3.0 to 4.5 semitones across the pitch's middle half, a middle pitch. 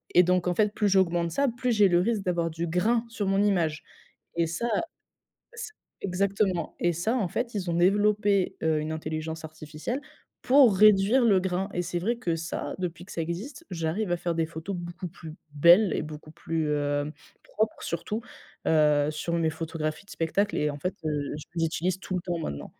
Yes: average, 4.1 semitones; medium, 175 Hz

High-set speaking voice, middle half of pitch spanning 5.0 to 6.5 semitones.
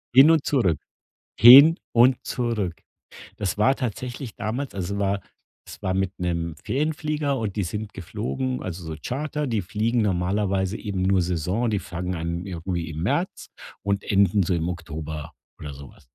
No: low, 100 Hz; wide, 5.5 semitones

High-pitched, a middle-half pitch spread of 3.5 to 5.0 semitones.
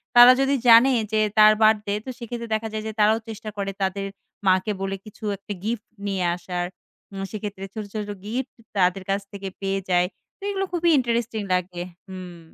No: high, 210 Hz; average, 2.9 semitones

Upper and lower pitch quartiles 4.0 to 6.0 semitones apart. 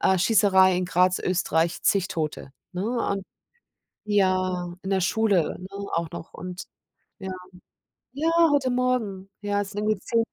No: average, 2.7 semitones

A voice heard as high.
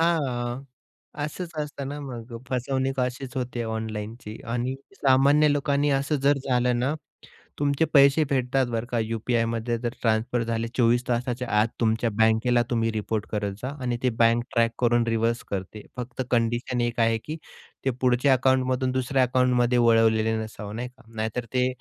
No: low, 125 Hz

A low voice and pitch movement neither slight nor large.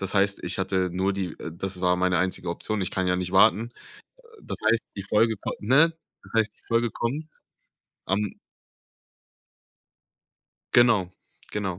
Yes: low, 100 Hz; average, 3.4 semitones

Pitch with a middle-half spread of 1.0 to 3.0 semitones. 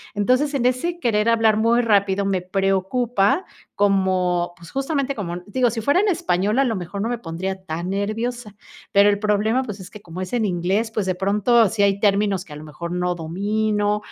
No: average, 3.5 semitones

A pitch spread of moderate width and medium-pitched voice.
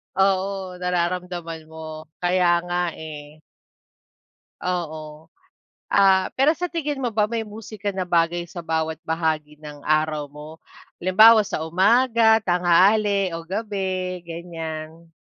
Yes: average, 3.7 semitones; medium, 175 Hz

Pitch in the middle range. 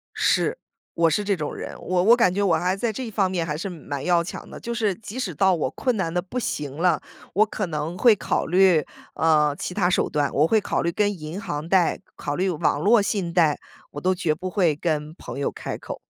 Yes: medium, 180 Hz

